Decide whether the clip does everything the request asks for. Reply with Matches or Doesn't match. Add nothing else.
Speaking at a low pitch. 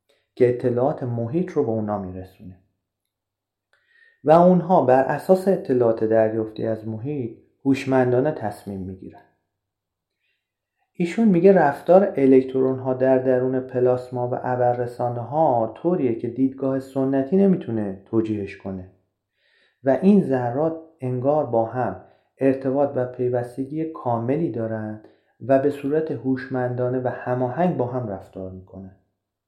Matches